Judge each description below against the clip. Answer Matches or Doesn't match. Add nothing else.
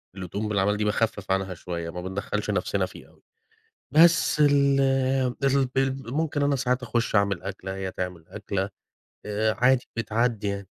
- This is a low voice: Matches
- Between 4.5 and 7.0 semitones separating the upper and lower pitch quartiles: Matches